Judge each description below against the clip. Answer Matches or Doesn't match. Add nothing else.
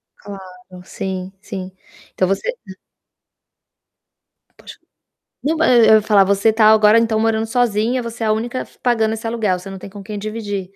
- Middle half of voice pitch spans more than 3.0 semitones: Doesn't match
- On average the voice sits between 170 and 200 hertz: Doesn't match